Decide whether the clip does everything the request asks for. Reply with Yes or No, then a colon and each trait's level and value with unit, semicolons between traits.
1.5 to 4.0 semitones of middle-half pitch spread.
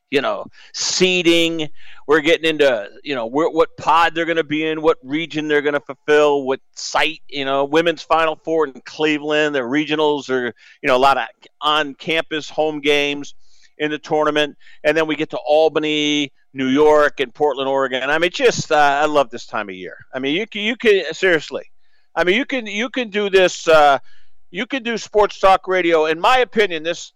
Yes: average, 2.9 semitones